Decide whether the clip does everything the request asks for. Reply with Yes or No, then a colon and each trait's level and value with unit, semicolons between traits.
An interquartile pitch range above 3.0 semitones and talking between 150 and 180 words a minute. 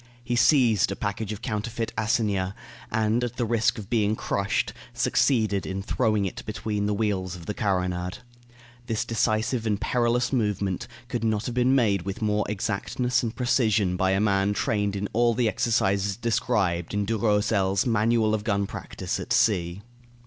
No: average, 2.7 semitones; average, 165 wpm